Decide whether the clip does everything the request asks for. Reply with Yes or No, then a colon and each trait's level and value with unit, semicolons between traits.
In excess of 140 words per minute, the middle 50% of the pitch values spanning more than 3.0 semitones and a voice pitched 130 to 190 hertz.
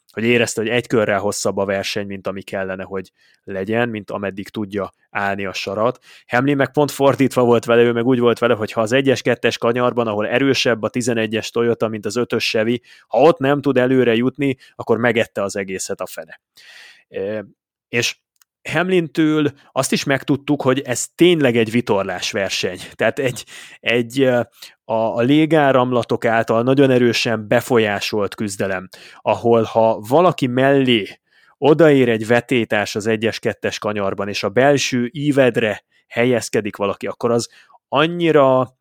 No: average, 150 wpm; average, 3.6 semitones; low, 120 Hz